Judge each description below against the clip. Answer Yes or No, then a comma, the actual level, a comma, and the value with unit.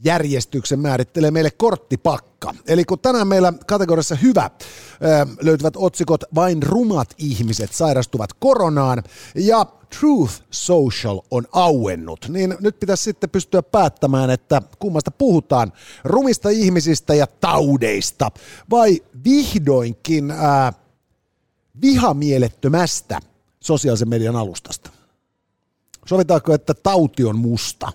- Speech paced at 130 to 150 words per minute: No, average, 100 wpm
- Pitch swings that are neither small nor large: No, wide, 6.2 semitones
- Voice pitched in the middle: Yes, medium, 155 Hz